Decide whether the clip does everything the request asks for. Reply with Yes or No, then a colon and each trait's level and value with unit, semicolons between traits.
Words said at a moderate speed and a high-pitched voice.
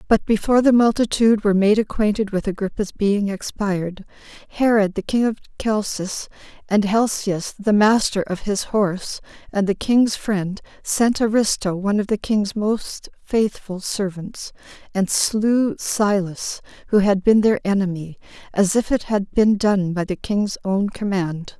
Yes: average, 155 wpm; high, 205 Hz